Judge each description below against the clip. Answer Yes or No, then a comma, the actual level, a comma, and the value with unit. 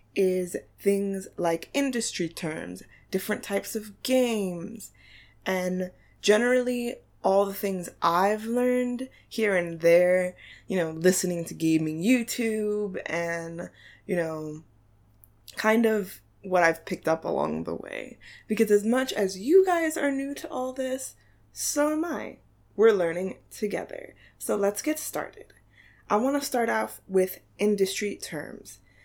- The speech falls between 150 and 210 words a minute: No, slow, 135 wpm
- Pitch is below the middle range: No, high, 195 Hz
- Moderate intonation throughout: No, wide, 5.8 semitones